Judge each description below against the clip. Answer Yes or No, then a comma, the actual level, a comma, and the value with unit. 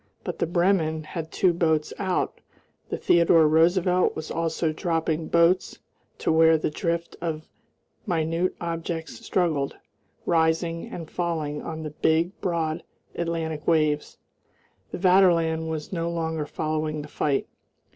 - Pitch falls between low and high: Yes, medium, 165 Hz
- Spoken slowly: Yes, slow, 130 wpm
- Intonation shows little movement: Yes, narrow, 1.4 semitones